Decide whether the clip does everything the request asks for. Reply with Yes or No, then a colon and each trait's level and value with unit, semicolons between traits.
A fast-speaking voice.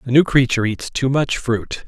Yes: fast, 225 wpm